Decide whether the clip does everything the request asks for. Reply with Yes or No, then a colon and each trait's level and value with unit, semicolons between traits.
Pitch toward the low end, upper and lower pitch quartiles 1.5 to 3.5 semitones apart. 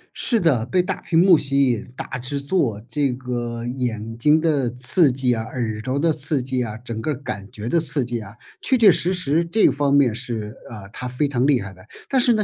No: low, 130 Hz; average, 4.6 semitones